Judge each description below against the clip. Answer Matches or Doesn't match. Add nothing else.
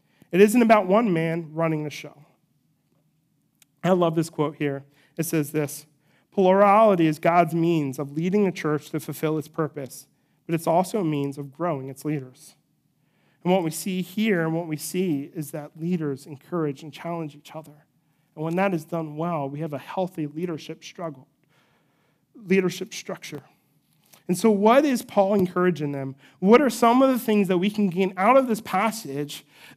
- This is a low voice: Doesn't match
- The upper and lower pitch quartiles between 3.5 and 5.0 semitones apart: Matches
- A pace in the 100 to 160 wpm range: Doesn't match